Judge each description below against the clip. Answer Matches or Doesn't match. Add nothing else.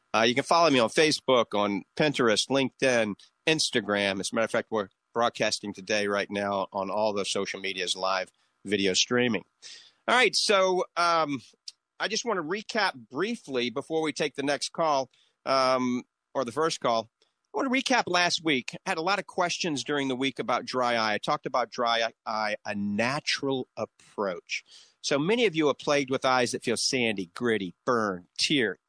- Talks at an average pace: Matches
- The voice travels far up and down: Matches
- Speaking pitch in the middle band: Doesn't match